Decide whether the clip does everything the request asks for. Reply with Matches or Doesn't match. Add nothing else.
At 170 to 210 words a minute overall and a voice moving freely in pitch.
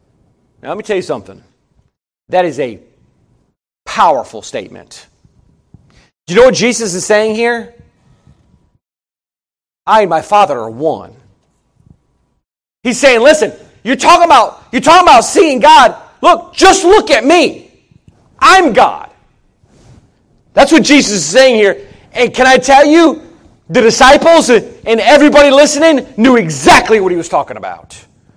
Doesn't match